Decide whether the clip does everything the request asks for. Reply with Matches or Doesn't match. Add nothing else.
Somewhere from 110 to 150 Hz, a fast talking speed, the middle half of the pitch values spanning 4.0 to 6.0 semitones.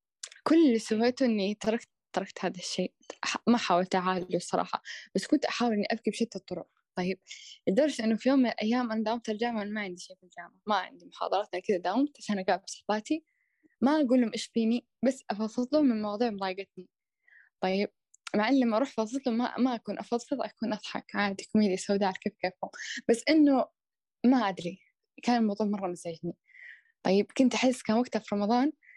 Doesn't match